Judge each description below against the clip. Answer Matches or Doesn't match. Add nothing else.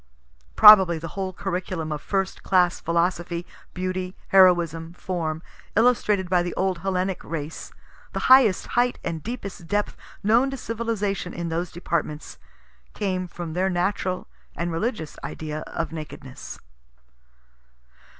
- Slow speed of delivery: Matches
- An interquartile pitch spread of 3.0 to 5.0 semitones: Doesn't match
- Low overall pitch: Doesn't match